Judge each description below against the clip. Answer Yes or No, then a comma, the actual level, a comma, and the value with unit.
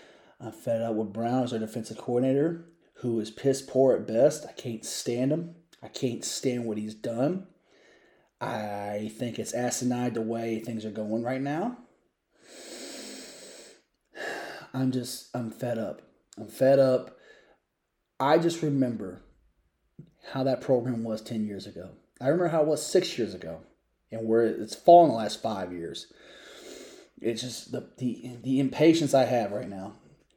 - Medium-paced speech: Yes, average, 160 wpm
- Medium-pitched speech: No, low, 120 Hz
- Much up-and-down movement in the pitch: No, average, 3.7 semitones